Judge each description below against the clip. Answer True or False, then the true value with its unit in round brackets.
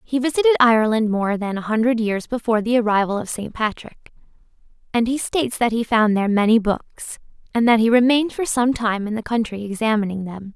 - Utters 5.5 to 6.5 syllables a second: True (5.9 syllables/s)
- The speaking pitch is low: False (225 Hz)